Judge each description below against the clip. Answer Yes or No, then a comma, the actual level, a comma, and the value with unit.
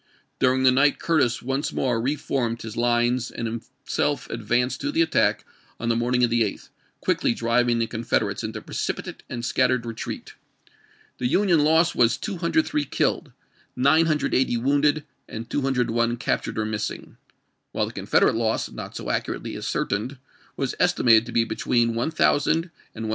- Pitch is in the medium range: No, low, 120 Hz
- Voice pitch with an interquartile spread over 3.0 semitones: Yes, average, 3.4 semitones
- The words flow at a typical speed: Yes, average, 155 wpm